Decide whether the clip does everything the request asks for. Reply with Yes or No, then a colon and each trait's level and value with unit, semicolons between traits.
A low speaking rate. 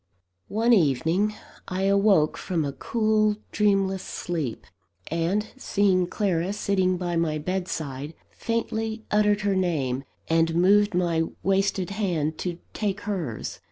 Yes: slow, 120 wpm